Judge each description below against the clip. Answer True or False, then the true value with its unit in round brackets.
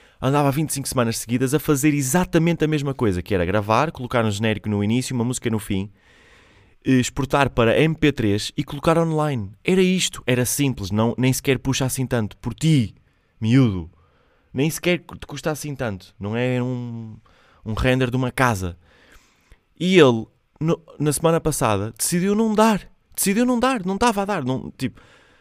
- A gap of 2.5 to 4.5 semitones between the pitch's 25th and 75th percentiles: False (5.4 semitones)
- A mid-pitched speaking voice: False (130 Hz)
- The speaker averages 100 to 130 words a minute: False (170 wpm)